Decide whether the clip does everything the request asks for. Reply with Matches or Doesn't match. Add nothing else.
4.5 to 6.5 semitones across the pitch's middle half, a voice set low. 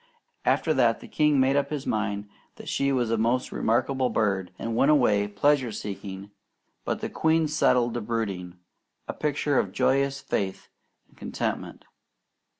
Matches